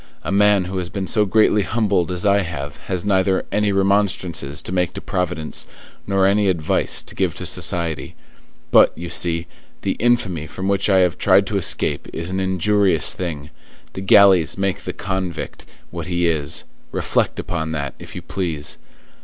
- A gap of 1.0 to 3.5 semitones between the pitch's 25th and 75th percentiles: Yes, average, 2.8 semitones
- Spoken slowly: No, average, 175 wpm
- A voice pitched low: Yes, very low, 95 Hz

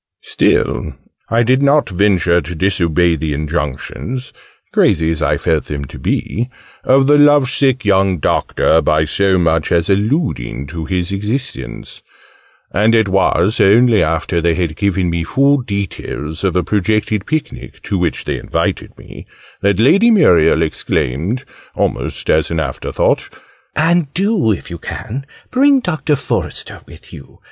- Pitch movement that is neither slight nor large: No, wide, 7.7 semitones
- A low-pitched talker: Yes, very low, 95 Hz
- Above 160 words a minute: No, average, 150 wpm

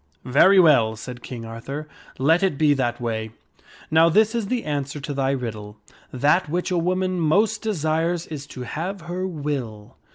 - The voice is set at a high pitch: No, medium, 150 Hz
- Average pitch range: No, wide, 6.0 semitones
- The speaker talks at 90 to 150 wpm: No, average, 170 wpm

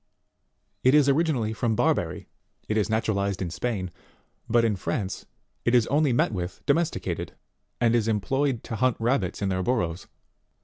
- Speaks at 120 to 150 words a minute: No, average, 165 wpm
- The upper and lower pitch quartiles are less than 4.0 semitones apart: No, average, 4.4 semitones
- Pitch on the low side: Yes, low, 115 Hz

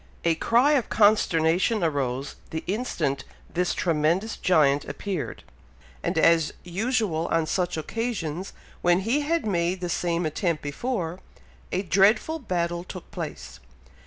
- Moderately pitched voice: Yes, medium, 175 Hz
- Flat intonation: No, average, 4.7 semitones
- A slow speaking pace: Yes, slow, 130 wpm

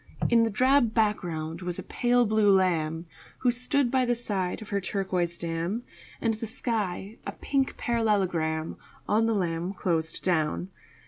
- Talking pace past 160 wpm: No, average, 155 wpm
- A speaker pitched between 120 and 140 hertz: No, high, 200 Hz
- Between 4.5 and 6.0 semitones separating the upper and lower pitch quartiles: Yes, average, 5.0 semitones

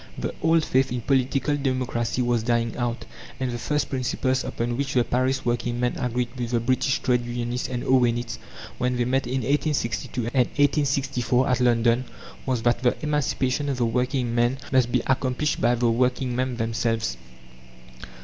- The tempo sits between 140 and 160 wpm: No, average, 170 wpm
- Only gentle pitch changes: Yes, narrow, 1.7 semitones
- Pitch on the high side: No, low, 125 Hz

